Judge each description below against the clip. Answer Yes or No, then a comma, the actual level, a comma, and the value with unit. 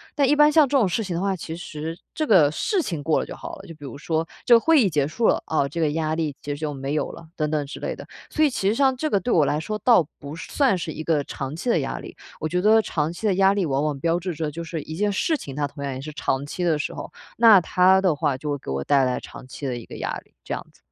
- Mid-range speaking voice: Yes, medium, 165 Hz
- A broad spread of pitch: Yes, wide, 6.0 semitones